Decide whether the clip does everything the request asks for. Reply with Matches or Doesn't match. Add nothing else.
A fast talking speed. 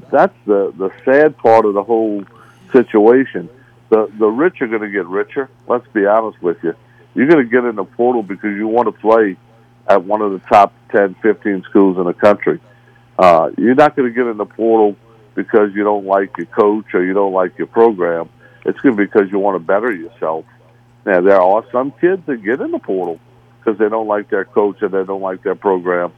Matches